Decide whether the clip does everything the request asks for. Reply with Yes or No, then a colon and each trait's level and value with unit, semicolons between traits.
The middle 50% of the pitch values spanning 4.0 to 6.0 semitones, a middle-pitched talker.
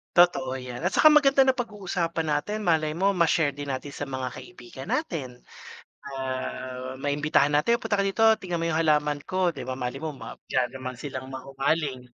Yes: average, 5.3 semitones; medium, 150 Hz